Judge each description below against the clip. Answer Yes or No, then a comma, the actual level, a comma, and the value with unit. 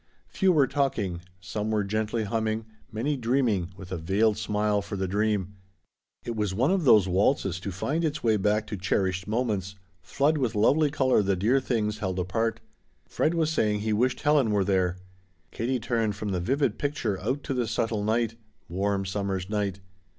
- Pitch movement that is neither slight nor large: Yes, average, 4.1 semitones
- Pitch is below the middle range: Yes, low, 105 Hz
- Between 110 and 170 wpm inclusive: No, average, 180 wpm